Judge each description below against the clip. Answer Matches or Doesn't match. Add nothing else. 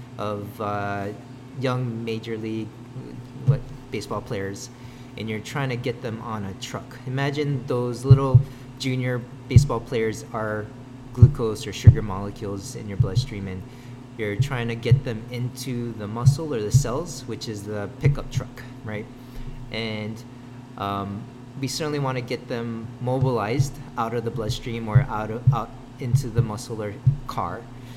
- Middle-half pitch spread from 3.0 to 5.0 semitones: Doesn't match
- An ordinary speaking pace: Matches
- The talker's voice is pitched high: Doesn't match